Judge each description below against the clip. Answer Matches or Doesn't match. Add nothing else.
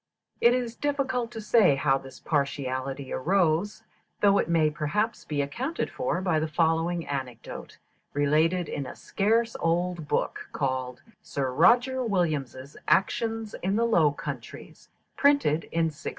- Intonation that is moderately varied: Doesn't match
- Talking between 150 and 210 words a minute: Doesn't match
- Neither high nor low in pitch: Matches